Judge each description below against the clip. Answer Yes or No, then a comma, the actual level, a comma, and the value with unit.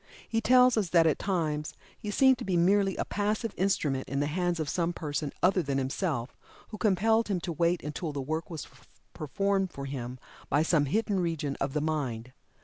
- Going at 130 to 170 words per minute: No, average, 200 wpm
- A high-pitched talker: No, medium, 170 Hz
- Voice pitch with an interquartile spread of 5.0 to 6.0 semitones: Yes, average, 5.3 semitones